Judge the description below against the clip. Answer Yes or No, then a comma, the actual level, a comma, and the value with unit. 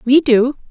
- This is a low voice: No, very high, 260 Hz